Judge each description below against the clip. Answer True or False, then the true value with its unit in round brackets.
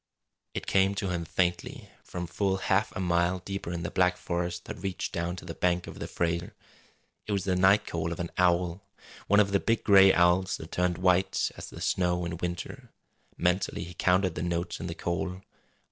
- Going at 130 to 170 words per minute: False (205 wpm)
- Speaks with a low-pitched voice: True (90 Hz)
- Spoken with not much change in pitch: True (1.6 semitones)